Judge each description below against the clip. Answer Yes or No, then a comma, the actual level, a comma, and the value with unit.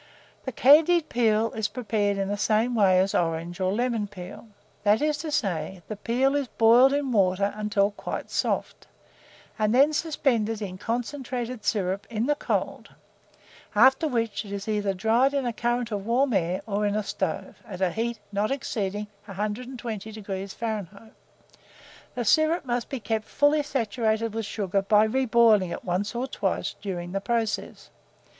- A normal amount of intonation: Yes, average, 3.6 semitones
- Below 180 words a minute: Yes, average, 165 wpm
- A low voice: No, high, 220 Hz